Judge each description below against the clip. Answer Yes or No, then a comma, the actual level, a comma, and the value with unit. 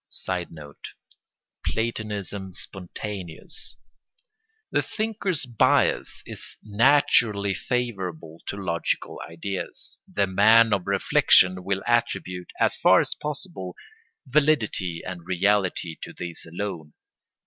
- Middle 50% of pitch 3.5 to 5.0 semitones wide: Yes, average, 4.3 semitones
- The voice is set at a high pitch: No, low, 100 Hz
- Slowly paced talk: Yes, slow, 95 wpm